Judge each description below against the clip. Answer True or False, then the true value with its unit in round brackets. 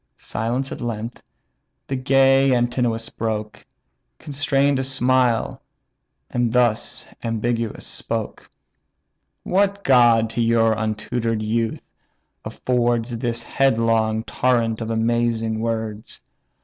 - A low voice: True (115 Hz)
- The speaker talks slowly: True (95 wpm)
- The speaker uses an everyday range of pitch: False (2.1 semitones)